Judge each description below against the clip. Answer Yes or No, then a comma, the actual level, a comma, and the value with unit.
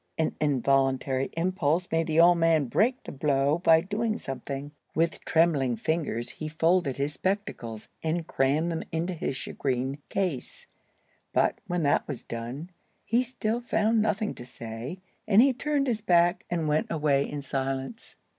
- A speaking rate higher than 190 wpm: No, average, 155 wpm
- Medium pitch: Yes, medium, 160 Hz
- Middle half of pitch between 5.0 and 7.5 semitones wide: Yes, average, 5.3 semitones